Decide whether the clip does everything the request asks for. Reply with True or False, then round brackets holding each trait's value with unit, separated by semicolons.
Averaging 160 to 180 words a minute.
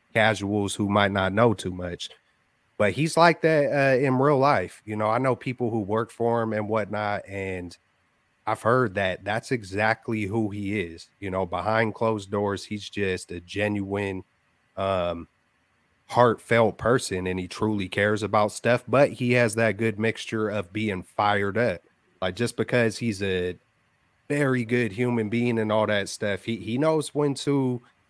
True (175 wpm)